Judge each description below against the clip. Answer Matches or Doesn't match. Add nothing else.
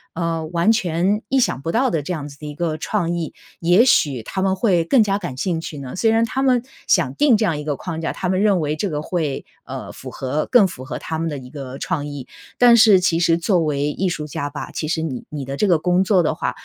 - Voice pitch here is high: Doesn't match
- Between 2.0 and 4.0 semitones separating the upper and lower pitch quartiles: Doesn't match